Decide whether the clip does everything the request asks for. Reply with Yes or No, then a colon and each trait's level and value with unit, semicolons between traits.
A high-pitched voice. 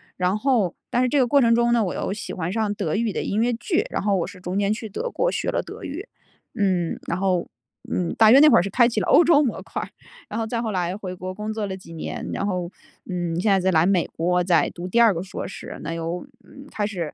Yes: high, 200 Hz